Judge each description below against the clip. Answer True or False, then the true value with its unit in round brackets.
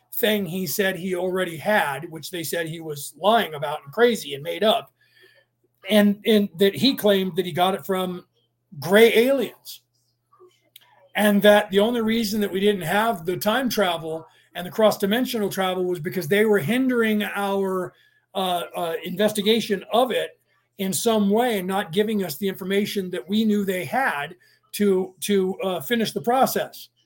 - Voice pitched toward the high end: True (200 Hz)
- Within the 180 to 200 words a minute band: False (170 wpm)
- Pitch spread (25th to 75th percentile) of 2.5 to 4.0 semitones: True (3.0 semitones)